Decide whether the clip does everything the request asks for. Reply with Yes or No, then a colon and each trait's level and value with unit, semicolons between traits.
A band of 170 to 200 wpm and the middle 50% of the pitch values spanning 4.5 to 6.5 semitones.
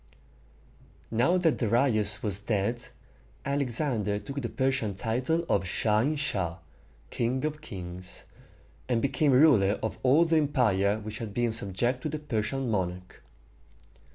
No: slow, 135 wpm; average, 5.2 semitones